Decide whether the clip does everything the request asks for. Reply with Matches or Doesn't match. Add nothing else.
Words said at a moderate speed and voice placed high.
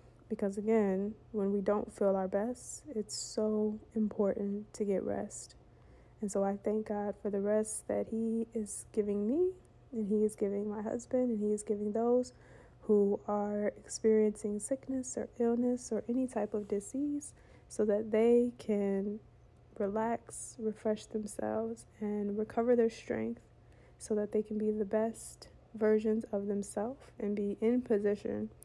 Matches